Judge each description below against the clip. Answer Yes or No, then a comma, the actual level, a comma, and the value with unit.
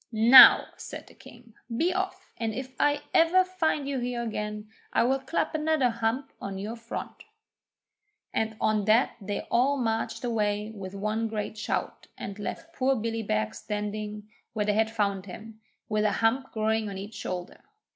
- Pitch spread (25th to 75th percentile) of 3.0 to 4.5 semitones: Yes, average, 3.5 semitones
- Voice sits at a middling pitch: No, high, 225 Hz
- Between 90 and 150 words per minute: No, average, 175 wpm